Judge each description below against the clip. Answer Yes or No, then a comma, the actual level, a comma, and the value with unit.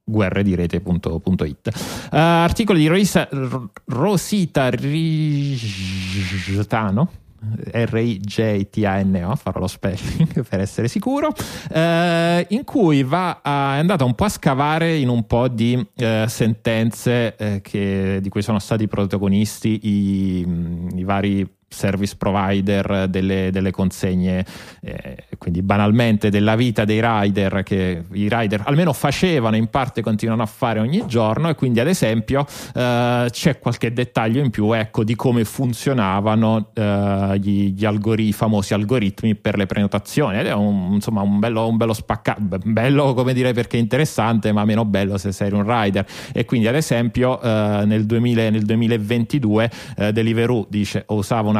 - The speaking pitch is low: Yes, low, 110 Hz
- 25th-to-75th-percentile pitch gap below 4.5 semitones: Yes, average, 3.9 semitones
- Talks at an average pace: Yes, average, 135 wpm